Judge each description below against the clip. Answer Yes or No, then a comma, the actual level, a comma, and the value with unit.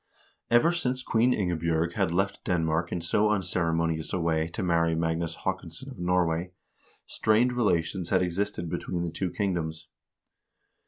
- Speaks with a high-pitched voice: No, very low, 85 Hz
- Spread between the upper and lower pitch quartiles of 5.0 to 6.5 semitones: No, average, 3.4 semitones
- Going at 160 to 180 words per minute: No, average, 145 wpm